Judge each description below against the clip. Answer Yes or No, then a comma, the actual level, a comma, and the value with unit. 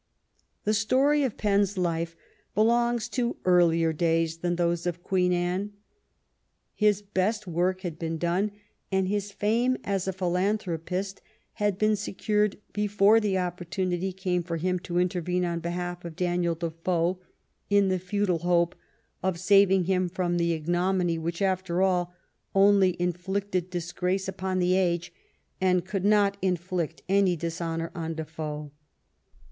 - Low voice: No, medium, 180 Hz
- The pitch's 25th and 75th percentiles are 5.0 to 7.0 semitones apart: No, narrow, 2.5 semitones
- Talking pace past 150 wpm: No, average, 140 wpm